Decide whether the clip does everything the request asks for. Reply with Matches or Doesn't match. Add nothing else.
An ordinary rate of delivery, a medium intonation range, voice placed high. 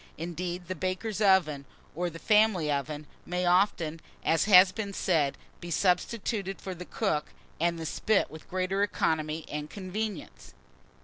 Doesn't match